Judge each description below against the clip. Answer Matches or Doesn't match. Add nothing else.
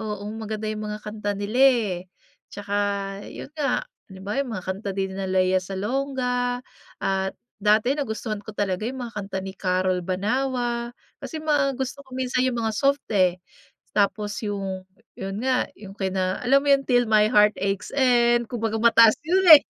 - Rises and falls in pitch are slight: Doesn't match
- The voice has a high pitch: Matches